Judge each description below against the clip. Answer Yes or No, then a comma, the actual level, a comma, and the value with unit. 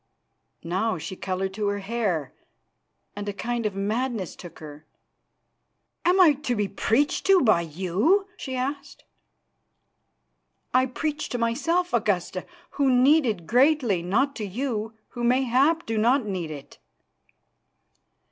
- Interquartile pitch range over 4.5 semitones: Yes, wide, 5.6 semitones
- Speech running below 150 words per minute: Yes, slow, 135 wpm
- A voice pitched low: No, high, 230 Hz